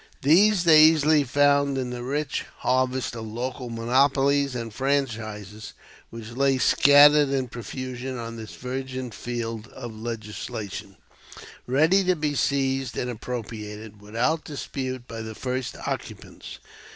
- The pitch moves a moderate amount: Yes, average, 3.5 semitones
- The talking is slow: Yes, slow, 125 wpm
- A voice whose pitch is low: Yes, low, 130 Hz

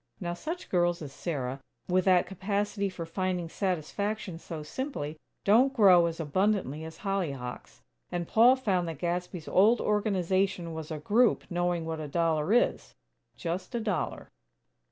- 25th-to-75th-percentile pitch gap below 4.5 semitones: Yes, average, 3.7 semitones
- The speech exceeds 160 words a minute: No, average, 150 wpm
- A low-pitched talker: No, medium, 180 Hz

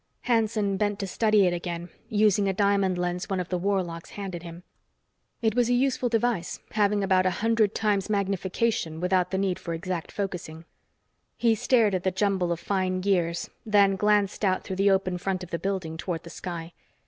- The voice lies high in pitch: Yes, high, 195 Hz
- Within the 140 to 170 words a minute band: No, average, 190 wpm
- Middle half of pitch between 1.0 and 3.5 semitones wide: Yes, narrow, 2.6 semitones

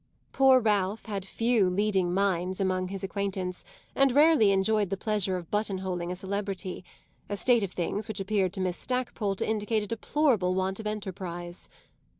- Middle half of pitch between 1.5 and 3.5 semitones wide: Yes, narrow, 2.5 semitones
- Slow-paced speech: No, average, 165 wpm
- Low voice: No, high, 195 Hz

